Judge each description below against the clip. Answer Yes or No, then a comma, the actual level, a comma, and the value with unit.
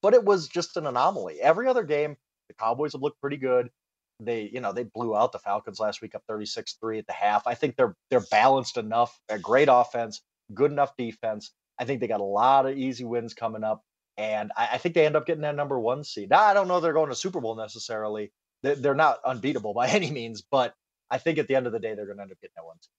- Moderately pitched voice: No, low, 125 Hz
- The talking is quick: Yes, fast, 265 wpm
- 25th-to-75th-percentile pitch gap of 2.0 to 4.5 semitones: No, average, 5.2 semitones